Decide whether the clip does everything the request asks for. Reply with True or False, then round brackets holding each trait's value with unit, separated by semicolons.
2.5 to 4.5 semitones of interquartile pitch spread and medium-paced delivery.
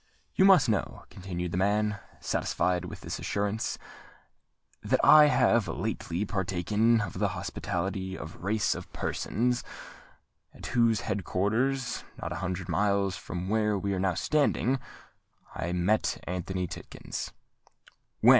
False (3.5 semitones; 130 wpm)